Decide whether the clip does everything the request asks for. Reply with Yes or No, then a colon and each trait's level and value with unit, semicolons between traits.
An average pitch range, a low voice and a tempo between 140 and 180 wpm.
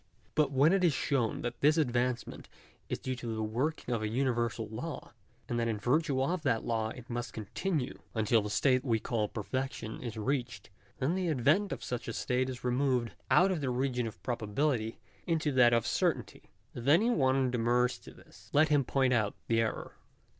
No: average, 3.4 semitones; low, 125 Hz; average, 195 wpm